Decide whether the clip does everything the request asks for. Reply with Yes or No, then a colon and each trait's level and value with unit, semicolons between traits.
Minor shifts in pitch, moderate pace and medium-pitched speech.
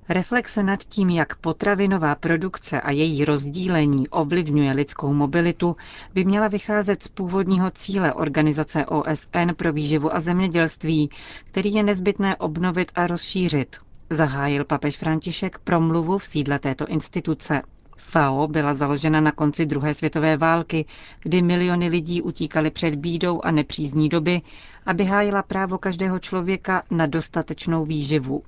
No: average, 3.3 semitones; average, 135 wpm; medium, 165 Hz